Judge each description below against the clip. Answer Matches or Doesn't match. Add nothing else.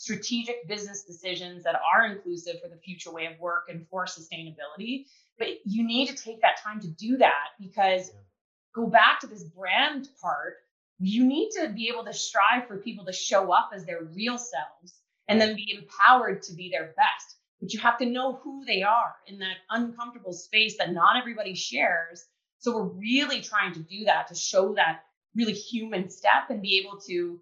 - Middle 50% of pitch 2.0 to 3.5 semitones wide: Doesn't match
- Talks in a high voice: Matches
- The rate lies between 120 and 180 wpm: Doesn't match